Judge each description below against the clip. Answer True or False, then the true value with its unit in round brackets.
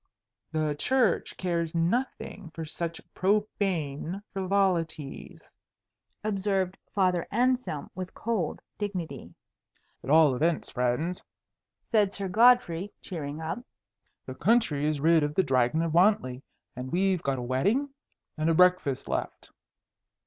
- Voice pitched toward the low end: False (170 Hz)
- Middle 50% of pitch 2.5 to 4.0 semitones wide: False (4.5 semitones)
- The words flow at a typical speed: False (120 wpm)